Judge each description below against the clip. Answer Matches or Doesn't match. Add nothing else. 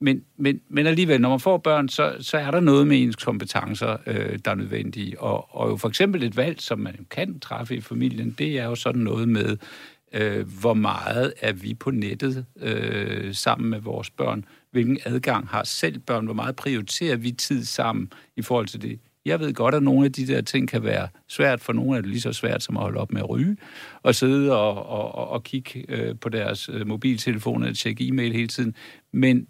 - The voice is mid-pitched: Doesn't match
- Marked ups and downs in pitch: Doesn't match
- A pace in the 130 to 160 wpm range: Doesn't match